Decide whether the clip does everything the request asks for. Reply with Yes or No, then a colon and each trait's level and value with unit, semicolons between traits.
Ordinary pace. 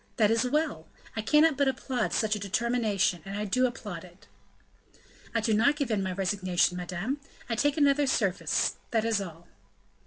Yes: average, 180 wpm